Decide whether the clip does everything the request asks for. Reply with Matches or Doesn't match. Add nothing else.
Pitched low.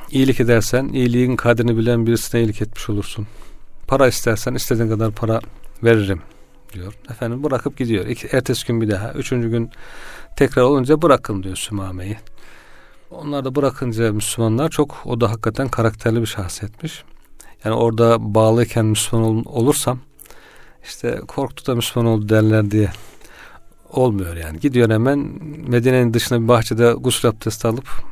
Matches